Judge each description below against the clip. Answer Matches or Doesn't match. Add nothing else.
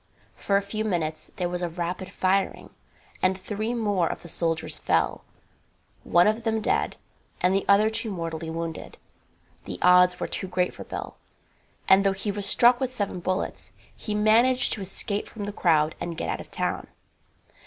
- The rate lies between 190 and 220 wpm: Doesn't match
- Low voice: Doesn't match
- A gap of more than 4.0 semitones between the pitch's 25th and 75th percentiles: Doesn't match